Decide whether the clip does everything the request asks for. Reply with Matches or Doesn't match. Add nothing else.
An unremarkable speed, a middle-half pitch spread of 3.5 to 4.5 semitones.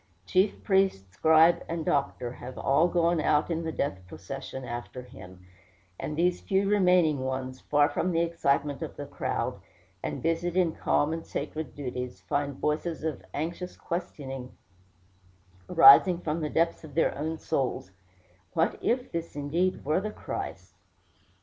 Matches